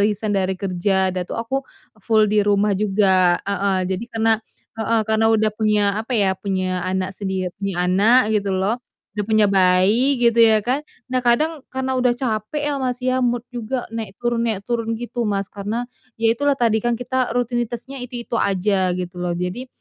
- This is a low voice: No, high, 215 Hz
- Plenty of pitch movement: No, average, 3.7 semitones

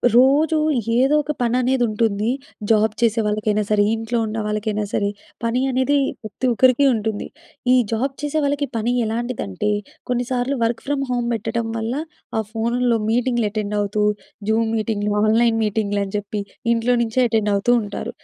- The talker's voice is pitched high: Yes, high, 225 Hz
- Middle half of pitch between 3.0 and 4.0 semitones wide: No, narrow, 2.6 semitones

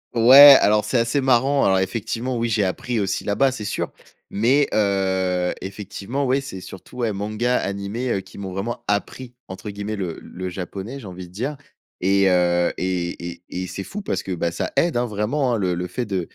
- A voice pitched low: Yes, low, 100 Hz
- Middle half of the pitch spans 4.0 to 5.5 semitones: Yes, average, 4.5 semitones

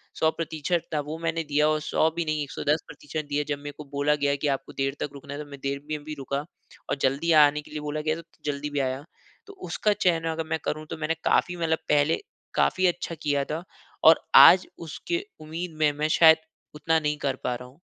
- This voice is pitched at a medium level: Yes, medium, 150 Hz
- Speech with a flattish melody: Yes, narrow, 2.0 semitones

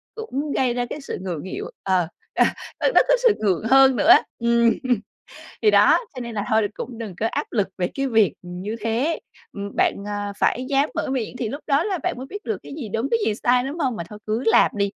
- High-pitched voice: Yes, high, 235 Hz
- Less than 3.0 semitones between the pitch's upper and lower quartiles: No, average, 4.7 semitones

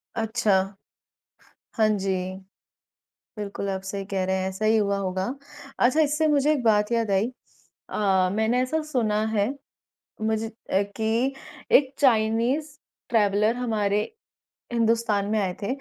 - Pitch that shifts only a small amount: No, average, 3.2 semitones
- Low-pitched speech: No, high, 220 Hz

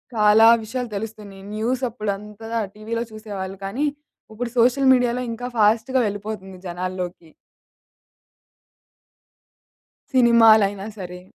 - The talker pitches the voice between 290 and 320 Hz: No, high, 215 Hz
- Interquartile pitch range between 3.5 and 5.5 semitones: No, average, 2.9 semitones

